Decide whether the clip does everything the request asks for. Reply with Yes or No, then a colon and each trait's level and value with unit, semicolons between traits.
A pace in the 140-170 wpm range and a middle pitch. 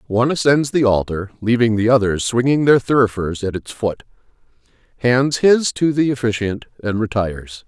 No: average, 150 wpm; low, 115 Hz